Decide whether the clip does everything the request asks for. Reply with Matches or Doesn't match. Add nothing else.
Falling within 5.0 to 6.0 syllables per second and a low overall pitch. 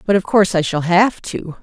Doesn't match